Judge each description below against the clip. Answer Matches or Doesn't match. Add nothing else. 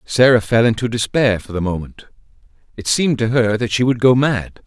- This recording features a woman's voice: Doesn't match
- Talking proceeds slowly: Doesn't match